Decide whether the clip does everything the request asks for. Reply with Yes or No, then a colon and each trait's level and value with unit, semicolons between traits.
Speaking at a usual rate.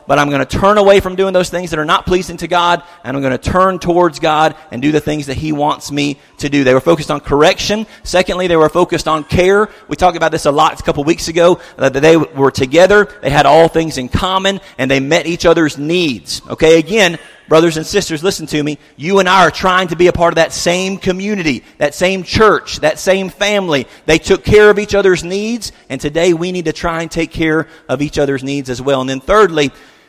No: fast, 245 wpm